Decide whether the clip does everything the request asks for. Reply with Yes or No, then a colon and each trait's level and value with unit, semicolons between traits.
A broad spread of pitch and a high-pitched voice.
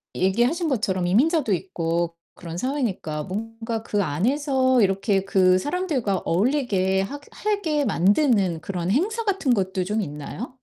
Yes: wide, 6.7 semitones; high, 210 Hz